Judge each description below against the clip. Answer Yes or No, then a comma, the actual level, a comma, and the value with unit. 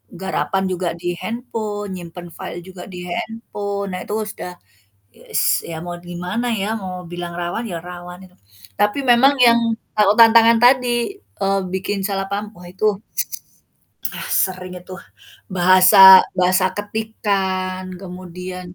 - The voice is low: No, high, 190 Hz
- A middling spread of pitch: Yes, average, 3.1 semitones